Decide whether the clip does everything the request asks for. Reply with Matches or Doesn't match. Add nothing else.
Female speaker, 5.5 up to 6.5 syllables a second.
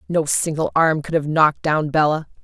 Doesn't match